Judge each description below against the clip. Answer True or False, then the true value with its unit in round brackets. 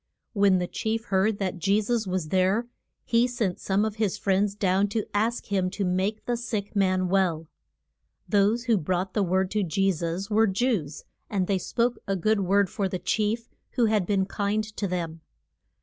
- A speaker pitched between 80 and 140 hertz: False (200 Hz)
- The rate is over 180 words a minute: True (190 wpm)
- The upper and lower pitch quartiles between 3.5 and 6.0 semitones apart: False (2.6 semitones)